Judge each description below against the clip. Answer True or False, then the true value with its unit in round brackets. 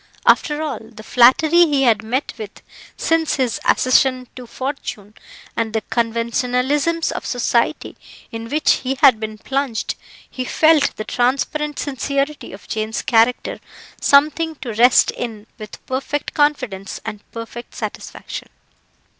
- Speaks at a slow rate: True (130 wpm)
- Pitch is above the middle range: True (255 Hz)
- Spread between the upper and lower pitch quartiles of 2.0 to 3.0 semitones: False (4.1 semitones)